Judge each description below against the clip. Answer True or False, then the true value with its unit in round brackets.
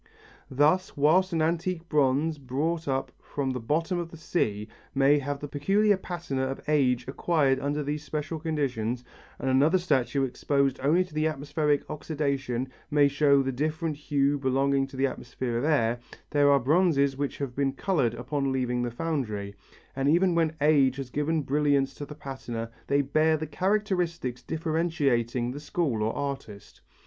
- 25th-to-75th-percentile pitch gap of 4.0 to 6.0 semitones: False (3.0 semitones)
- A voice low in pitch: False (145 Hz)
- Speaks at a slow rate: False (165 wpm)